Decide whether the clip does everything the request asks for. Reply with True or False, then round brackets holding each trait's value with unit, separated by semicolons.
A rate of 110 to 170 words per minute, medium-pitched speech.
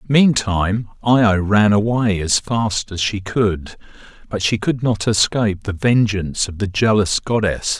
False (160 wpm; 105 Hz)